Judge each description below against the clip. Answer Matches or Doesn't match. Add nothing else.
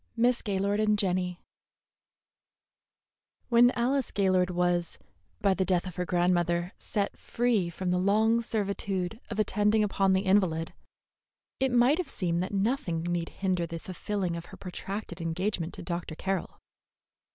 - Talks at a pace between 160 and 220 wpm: Doesn't match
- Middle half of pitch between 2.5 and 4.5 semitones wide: Matches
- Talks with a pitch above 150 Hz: Matches